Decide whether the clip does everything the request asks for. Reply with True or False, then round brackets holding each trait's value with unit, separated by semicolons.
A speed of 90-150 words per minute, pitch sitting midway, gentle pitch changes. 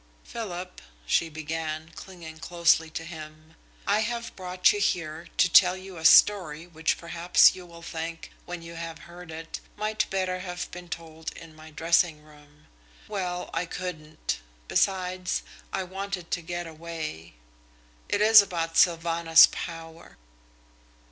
True (140 wpm; 170 Hz; 2.1 semitones)